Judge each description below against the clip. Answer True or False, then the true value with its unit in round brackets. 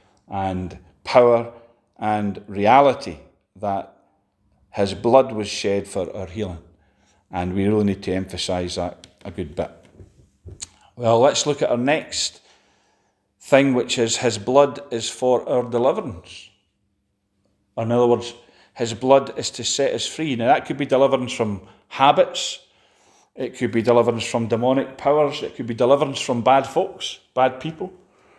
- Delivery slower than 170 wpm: True (150 wpm)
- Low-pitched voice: True (115 Hz)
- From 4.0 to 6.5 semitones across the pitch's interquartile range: True (4.5 semitones)